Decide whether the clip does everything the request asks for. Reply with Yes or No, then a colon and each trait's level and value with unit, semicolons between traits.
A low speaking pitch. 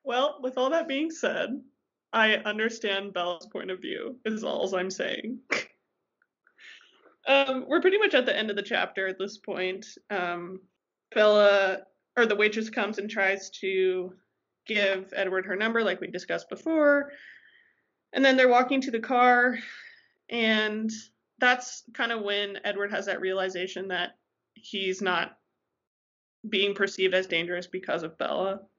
No: high, 215 Hz